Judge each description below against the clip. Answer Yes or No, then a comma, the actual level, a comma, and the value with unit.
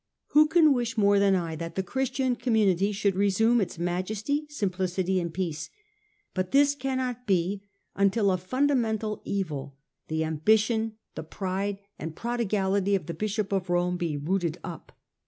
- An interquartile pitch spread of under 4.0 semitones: No, average, 4.3 semitones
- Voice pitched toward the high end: Yes, high, 200 Hz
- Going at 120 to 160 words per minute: Yes, average, 155 wpm